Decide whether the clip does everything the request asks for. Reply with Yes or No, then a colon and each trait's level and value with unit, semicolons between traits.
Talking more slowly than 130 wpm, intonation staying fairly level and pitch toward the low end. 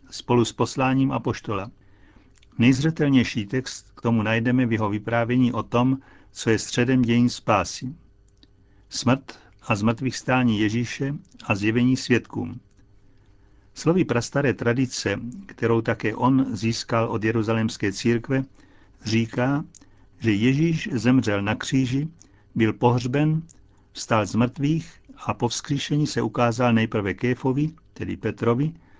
No: average, 120 wpm; average, 3.4 semitones; low, 120 Hz